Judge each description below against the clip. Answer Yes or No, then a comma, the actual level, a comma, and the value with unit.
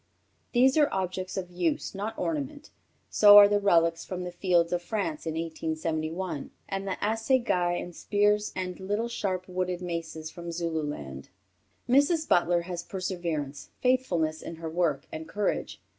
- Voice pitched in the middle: Yes, medium, 180 Hz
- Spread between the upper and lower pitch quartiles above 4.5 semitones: No, average, 3.7 semitones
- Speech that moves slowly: No, average, 150 wpm